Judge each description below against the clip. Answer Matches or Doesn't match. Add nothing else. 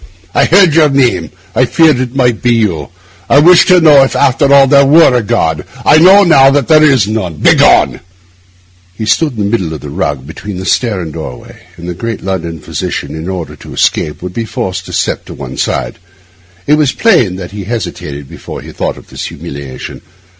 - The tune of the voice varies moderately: Doesn't match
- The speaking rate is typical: Doesn't match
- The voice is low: Matches